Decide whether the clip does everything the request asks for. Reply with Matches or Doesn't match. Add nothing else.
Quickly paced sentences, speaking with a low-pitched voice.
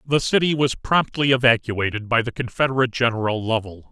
Doesn't match